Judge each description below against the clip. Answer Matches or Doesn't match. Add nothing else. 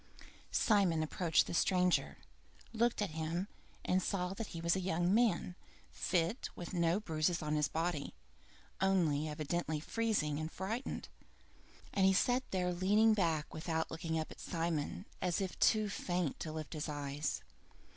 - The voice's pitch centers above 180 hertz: Doesn't match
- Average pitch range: Matches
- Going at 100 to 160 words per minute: Matches